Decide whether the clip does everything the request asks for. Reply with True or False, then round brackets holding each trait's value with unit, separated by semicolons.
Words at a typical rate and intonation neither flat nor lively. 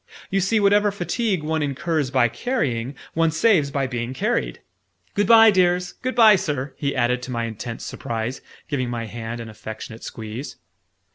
False (165 wpm; 7.9 semitones)